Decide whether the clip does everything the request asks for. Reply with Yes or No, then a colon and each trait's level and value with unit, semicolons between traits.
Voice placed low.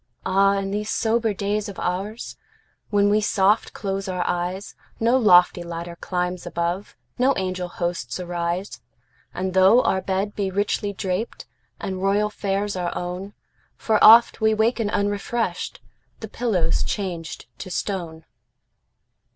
No: high, 195 Hz